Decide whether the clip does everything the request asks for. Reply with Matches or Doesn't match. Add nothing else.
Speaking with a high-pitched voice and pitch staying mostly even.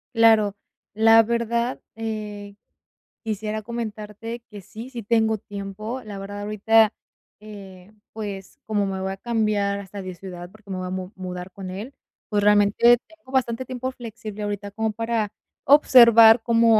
Matches